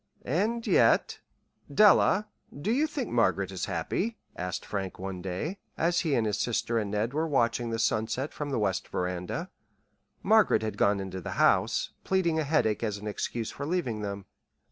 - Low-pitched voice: Yes, low, 115 Hz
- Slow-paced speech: No, average, 175 wpm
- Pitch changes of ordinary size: No, wide, 8.3 semitones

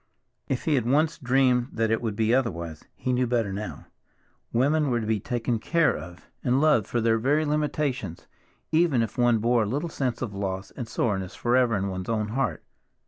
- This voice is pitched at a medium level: No, low, 120 Hz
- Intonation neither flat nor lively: Yes, average, 3.8 semitones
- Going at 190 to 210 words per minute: Yes, average, 195 wpm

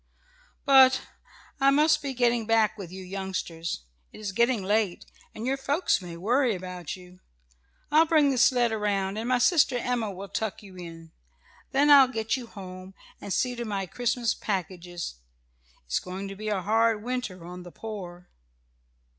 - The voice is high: Yes, high, 215 Hz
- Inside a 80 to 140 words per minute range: No, average, 170 wpm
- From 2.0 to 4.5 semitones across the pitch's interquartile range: No, average, 5.1 semitones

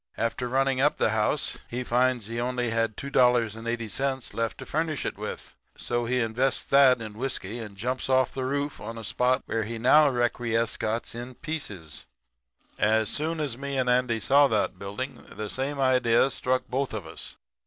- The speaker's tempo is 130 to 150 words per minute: No, average, 175 wpm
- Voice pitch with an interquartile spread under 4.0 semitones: Yes, average, 2.8 semitones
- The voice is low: Yes, low, 125 Hz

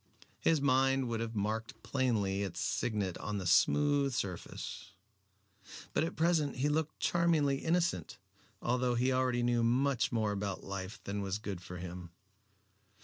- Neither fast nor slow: Yes, average, 145 wpm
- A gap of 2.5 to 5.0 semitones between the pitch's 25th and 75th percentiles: No, wide, 5.6 semitones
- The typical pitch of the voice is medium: No, low, 120 Hz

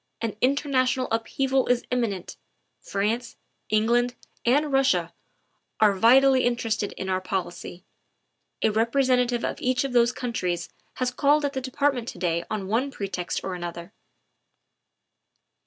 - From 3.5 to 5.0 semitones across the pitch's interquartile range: Yes, average, 4.4 semitones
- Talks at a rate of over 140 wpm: No, slow, 135 wpm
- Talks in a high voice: Yes, high, 240 Hz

